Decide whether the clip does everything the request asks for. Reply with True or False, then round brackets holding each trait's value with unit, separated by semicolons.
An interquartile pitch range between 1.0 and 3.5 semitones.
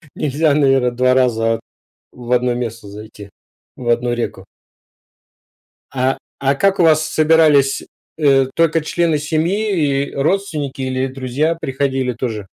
False (4.0 semitones)